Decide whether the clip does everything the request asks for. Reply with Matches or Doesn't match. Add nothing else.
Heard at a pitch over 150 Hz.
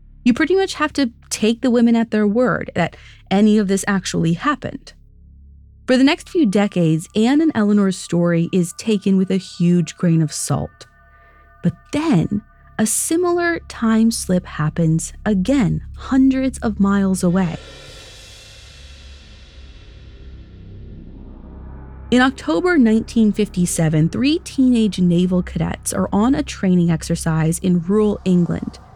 Matches